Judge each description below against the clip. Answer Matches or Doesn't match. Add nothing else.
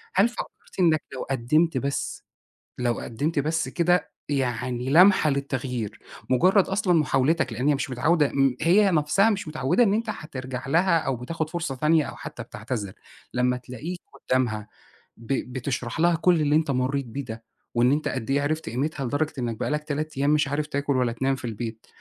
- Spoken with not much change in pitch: Doesn't match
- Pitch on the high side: Doesn't match